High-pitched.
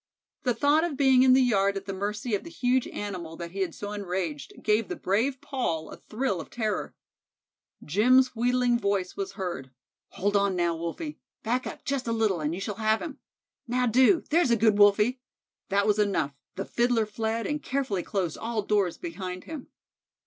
Yes: high, 210 Hz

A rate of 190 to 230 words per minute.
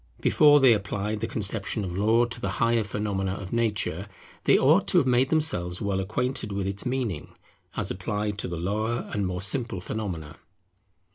No: average, 180 wpm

